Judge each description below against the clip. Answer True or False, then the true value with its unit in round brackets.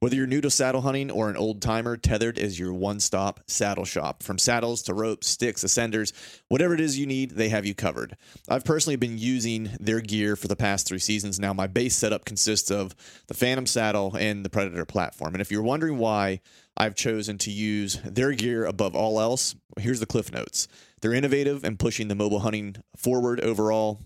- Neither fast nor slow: False (210 wpm)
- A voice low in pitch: True (110 Hz)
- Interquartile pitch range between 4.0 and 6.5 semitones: False (3.0 semitones)